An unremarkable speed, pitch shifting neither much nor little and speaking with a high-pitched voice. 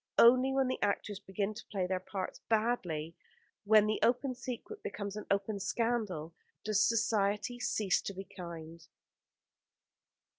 Yes: average, 145 wpm; average, 3.7 semitones; high, 210 Hz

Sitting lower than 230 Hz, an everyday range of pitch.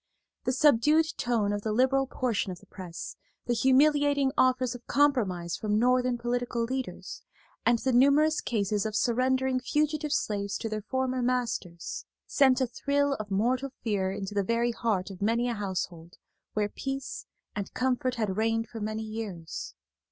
No: high, 240 Hz; average, 4.0 semitones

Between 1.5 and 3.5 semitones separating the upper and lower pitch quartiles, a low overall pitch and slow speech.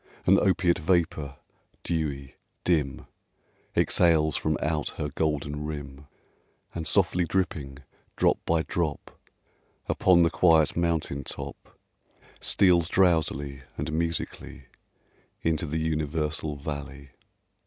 Yes: average, 2.7 semitones; very low, 80 Hz; slow, 100 wpm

